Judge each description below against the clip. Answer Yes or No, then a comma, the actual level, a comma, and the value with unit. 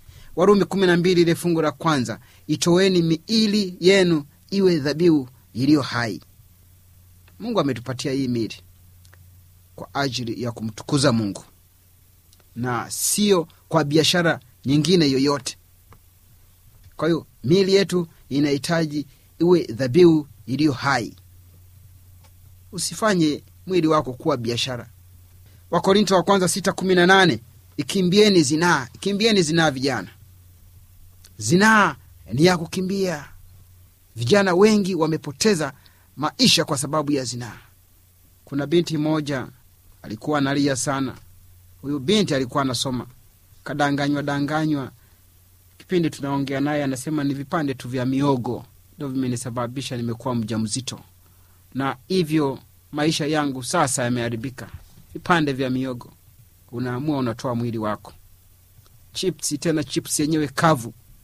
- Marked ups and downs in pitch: Yes, wide, 8.2 semitones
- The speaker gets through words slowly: Yes, slow, 95 wpm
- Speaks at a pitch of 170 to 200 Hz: No, low, 135 Hz